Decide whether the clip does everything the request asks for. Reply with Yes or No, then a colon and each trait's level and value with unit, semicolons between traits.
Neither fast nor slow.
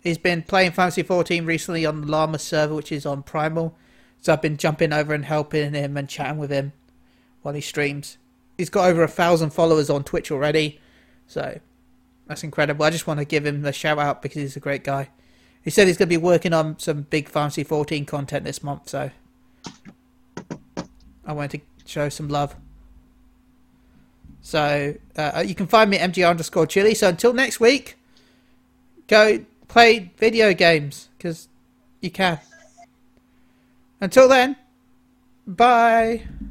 Yes: average, 165 wpm